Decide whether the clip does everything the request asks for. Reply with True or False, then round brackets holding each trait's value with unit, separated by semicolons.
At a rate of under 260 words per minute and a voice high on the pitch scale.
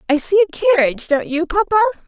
True (200 wpm; 345 Hz)